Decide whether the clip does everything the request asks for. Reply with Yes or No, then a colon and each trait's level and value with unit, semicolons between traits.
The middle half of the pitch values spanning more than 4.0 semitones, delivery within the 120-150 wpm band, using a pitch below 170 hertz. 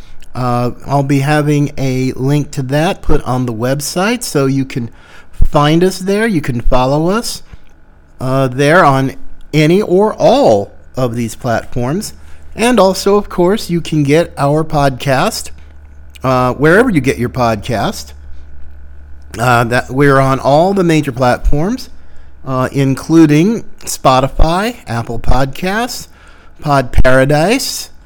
Yes: wide, 5.5 semitones; slow, 135 wpm; low, 135 Hz